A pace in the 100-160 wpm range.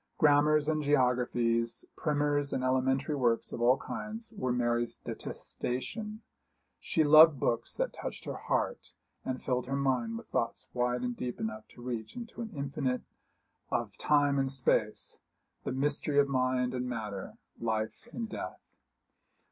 Yes: average, 150 wpm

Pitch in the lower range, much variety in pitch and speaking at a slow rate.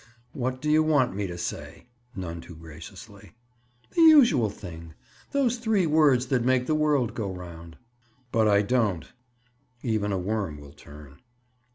No: low, 110 Hz; wide, 8.3 semitones; average, 155 wpm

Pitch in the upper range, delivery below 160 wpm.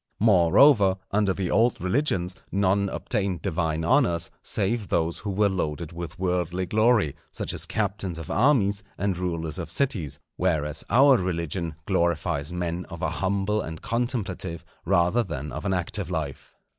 No: very low, 95 Hz; average, 150 wpm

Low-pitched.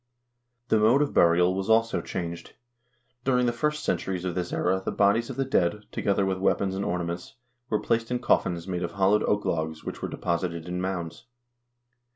Yes: very low, 95 Hz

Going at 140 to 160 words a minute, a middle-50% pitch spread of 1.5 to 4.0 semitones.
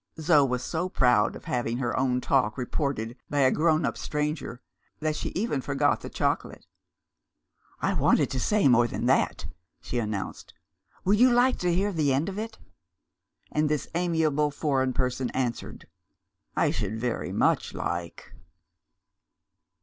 No: average, 150 wpm; average, 4.7 semitones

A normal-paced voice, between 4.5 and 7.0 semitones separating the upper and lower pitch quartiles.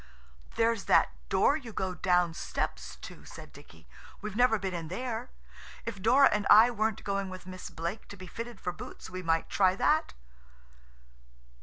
No: average, 170 wpm; average, 3.8 semitones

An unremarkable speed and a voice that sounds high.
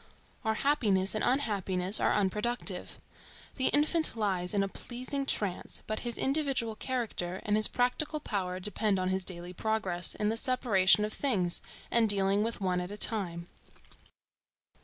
Yes: average, 155 wpm; high, 210 Hz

